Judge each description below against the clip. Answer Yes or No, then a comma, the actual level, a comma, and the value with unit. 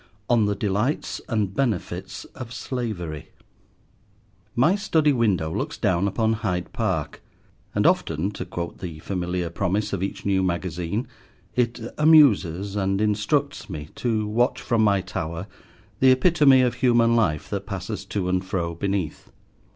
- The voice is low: Yes, low, 100 Hz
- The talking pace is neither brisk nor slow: Yes, average, 145 wpm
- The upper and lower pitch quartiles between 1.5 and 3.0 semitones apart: No, average, 4.8 semitones